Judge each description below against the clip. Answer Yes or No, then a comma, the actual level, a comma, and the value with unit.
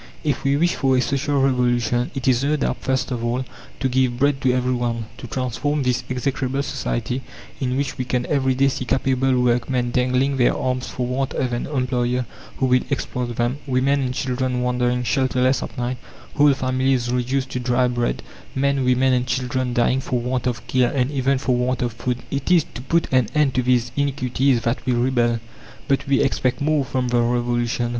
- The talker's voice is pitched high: No, low, 130 Hz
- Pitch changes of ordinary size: No, narrow, 1.5 semitones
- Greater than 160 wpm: Yes, average, 195 wpm